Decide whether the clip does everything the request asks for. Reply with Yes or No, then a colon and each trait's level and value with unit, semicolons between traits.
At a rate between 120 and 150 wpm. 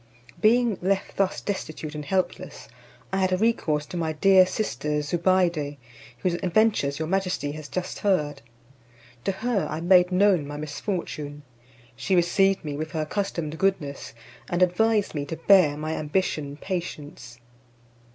Yes: average, 140 wpm